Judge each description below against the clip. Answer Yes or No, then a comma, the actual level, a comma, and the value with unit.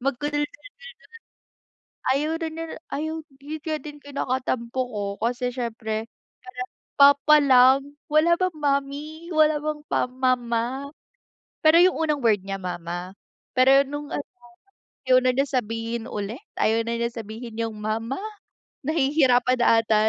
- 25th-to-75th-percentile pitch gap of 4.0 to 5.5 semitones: Yes, average, 4.3 semitones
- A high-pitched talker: Yes, very high, 260 Hz